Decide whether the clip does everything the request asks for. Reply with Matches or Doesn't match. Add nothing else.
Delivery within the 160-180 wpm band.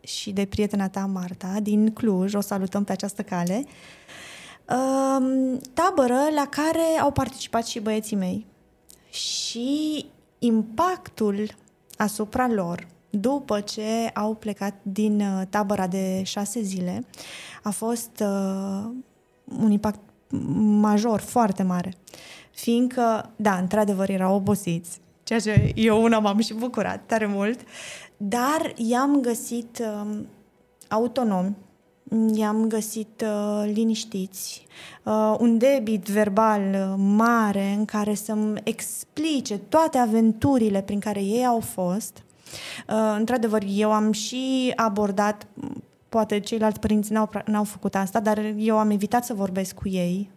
Doesn't match